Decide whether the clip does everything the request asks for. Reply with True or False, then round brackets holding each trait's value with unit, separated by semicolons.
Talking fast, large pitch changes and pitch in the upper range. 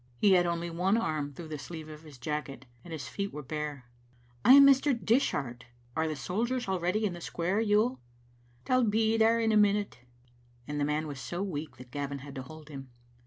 False (210 wpm; 6.5 semitones; 170 Hz)